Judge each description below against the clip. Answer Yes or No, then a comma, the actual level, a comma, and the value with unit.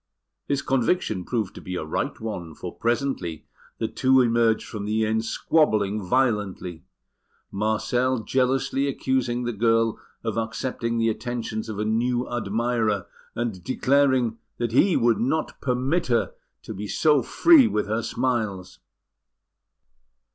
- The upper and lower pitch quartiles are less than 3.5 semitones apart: Yes, average, 3.1 semitones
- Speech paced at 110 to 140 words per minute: Yes, slow, 135 wpm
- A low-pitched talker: Yes, low, 115 Hz